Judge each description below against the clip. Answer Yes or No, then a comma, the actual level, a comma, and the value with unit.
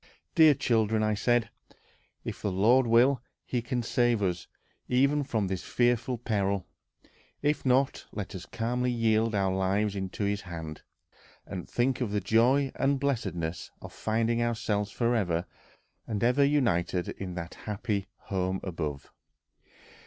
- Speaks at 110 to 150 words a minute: Yes, average, 140 wpm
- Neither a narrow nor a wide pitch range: Yes, average, 4.2 semitones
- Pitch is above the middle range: No, low, 110 Hz